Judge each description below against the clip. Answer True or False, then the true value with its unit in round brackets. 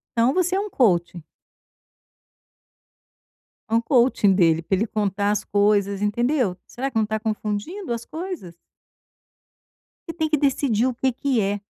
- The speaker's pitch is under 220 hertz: False (225 Hz)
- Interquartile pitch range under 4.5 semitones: False (5.1 semitones)